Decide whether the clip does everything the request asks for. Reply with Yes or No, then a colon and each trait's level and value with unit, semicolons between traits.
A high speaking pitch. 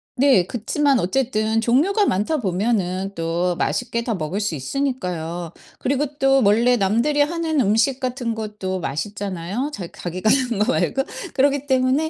Yes: high, 225 Hz